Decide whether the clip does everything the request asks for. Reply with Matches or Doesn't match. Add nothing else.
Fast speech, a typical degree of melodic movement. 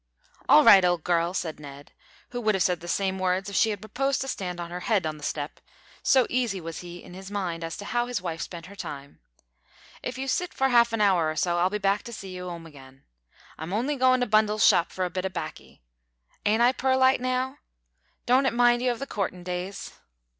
Doesn't match